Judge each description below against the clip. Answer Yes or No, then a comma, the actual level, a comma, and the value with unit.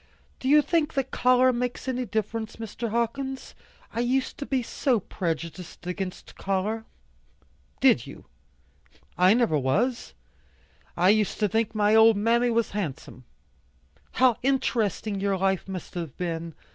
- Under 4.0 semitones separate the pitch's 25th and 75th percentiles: No, average, 4.6 semitones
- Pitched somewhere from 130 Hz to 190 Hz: No, high, 220 Hz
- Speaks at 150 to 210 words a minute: No, average, 140 wpm